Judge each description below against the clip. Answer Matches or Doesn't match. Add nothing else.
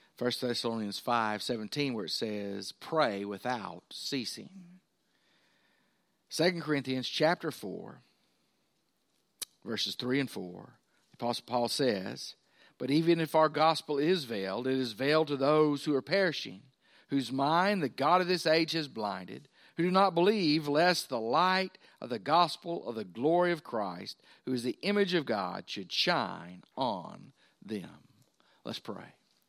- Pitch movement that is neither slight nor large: Doesn't match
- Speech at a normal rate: Matches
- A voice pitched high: Doesn't match